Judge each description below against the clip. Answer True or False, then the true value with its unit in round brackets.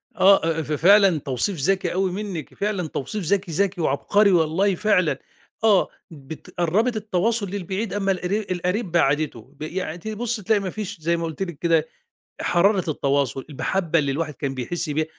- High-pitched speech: False (180 Hz)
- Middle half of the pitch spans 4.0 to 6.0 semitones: True (4.3 semitones)